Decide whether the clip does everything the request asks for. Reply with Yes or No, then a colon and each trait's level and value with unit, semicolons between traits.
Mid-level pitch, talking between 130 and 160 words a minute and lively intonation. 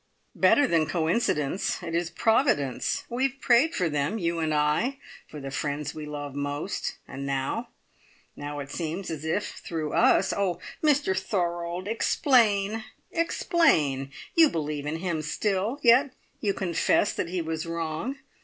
Yes: medium, 170 Hz; average, 150 wpm; wide, 6.5 semitones